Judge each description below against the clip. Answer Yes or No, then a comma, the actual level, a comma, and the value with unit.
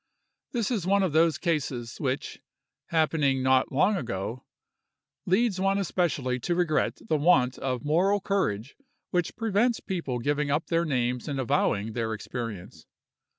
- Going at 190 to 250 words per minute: No, slow, 135 wpm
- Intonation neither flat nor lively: No, wide, 6.5 semitones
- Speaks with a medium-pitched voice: Yes, medium, 150 Hz